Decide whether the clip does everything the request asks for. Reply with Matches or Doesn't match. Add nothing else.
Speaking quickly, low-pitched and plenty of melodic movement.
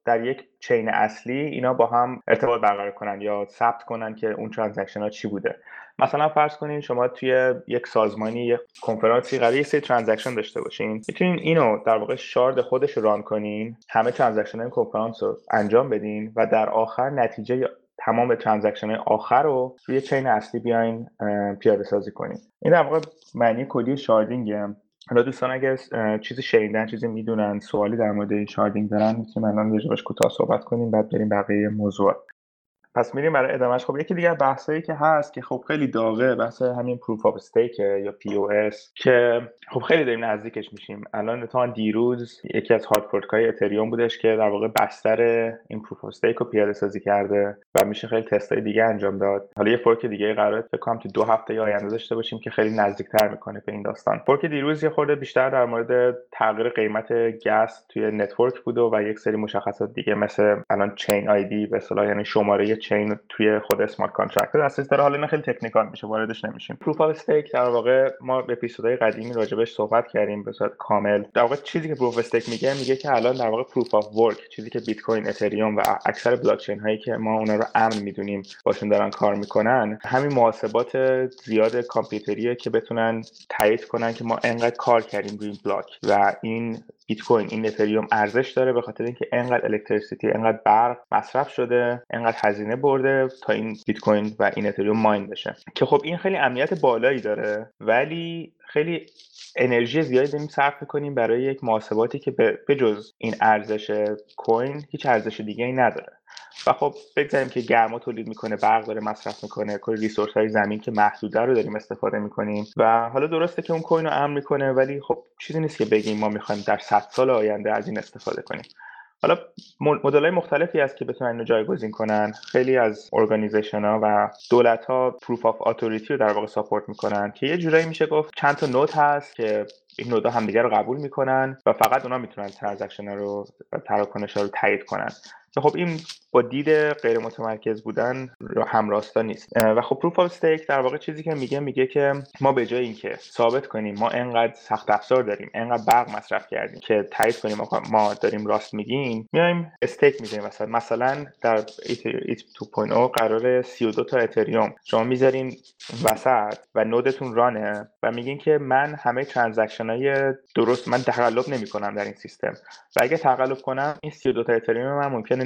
Doesn't match